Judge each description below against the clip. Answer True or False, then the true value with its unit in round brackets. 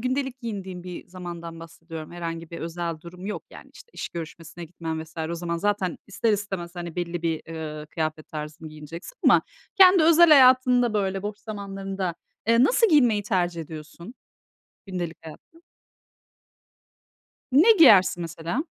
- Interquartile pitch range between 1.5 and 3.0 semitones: False (4.5 semitones)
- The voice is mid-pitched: True (180 Hz)